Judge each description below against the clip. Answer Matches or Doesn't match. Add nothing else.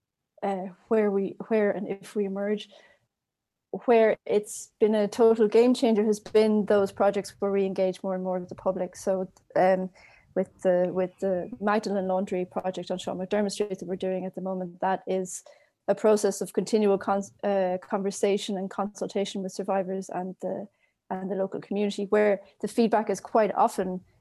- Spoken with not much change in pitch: Matches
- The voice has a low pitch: Doesn't match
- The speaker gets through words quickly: Doesn't match